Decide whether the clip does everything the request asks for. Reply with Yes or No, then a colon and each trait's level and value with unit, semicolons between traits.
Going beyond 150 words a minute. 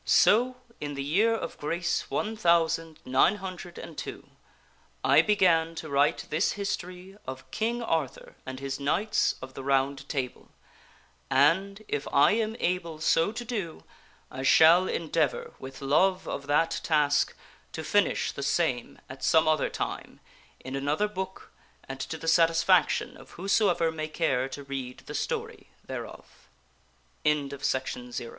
No: average, 145 wpm